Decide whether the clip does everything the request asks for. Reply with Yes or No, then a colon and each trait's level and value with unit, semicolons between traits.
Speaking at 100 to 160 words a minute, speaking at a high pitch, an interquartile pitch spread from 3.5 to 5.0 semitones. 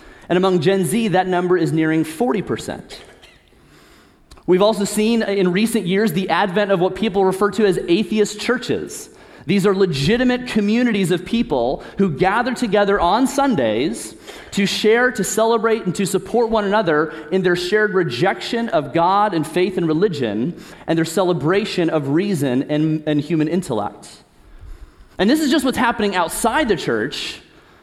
Yes: average, 155 wpm; high, 195 Hz; average, 4.1 semitones